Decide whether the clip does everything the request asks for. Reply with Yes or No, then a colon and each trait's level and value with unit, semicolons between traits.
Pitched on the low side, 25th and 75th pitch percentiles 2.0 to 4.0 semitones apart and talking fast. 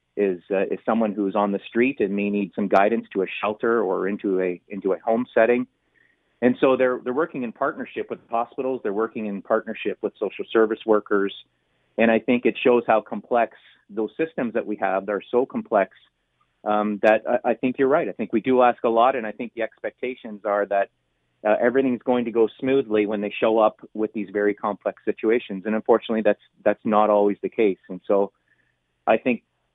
Yes: low, 110 Hz; average, 2.9 semitones; fast, 210 wpm